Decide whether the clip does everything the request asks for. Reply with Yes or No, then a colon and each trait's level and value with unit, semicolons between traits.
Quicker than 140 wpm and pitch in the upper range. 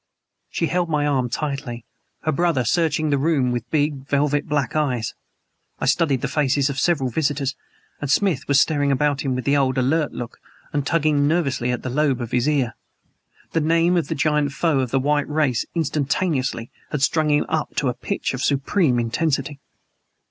No: average, 190 wpm; medium, 145 Hz